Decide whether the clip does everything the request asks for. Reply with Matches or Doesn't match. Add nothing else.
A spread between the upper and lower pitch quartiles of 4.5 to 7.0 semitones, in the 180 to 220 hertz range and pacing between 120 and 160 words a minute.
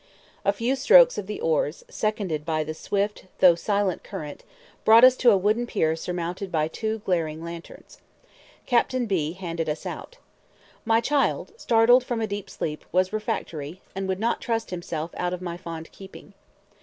Doesn't match